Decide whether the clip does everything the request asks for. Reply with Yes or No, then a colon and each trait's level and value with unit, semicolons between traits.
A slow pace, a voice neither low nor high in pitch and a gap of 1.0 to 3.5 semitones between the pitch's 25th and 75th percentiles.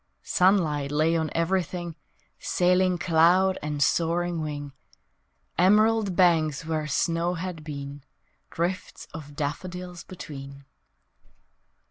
Yes: slow, 95 wpm; medium, 165 Hz; average, 3.2 semitones